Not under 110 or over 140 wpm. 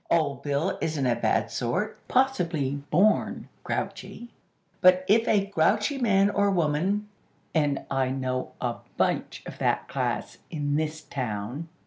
Yes: slow, 135 wpm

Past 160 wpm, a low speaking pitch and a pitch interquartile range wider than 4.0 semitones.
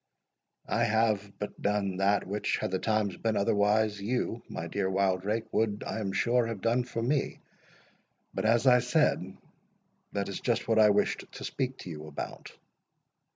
No: average, 170 wpm; low, 105 Hz; average, 2.7 semitones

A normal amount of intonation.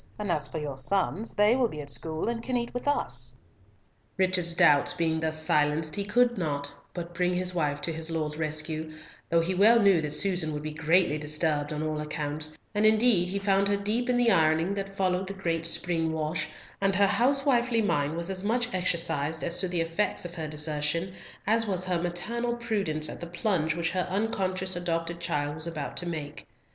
Yes: average, 4.2 semitones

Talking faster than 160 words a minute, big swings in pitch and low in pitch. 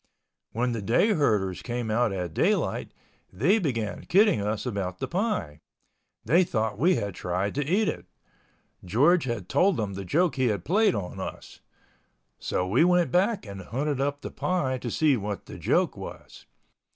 Yes: average, 175 wpm; wide, 9.0 semitones; low, 120 Hz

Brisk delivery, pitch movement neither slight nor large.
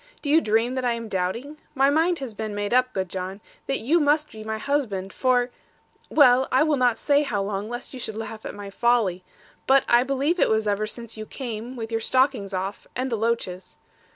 Yes: fast, 220 wpm; average, 4.1 semitones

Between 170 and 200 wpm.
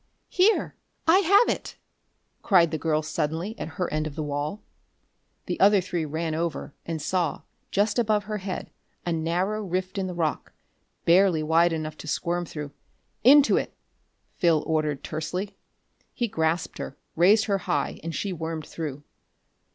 No: average, 160 wpm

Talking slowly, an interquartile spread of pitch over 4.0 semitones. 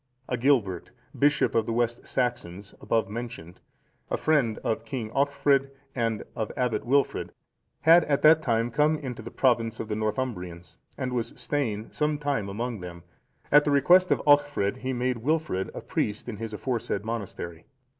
No: average, 165 wpm; average, 4.7 semitones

